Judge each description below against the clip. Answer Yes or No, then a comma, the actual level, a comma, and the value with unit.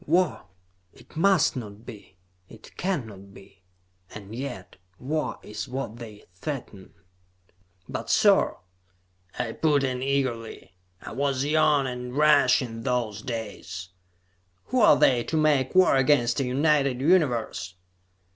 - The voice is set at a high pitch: No, low, 130 Hz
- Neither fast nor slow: No, slow, 125 wpm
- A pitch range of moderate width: Yes, average, 4.6 semitones